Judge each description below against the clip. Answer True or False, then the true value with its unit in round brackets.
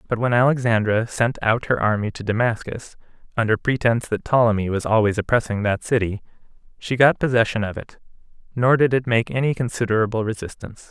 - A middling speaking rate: True (165 wpm)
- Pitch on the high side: False (115 Hz)